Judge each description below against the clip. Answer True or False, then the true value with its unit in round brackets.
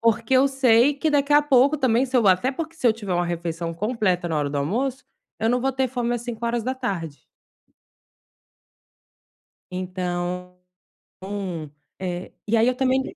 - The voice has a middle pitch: False (230 Hz)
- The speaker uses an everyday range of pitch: False (6.4 semitones)